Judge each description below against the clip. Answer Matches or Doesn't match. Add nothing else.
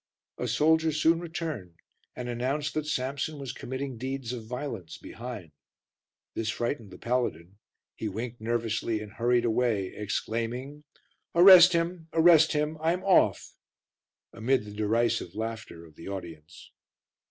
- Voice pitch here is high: Doesn't match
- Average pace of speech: Doesn't match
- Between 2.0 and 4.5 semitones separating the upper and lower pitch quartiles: Doesn't match